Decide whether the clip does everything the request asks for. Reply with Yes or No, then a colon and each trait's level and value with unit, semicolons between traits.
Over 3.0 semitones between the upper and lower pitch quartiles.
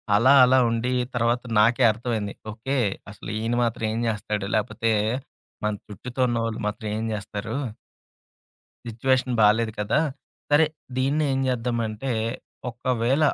No: average, 2.7 semitones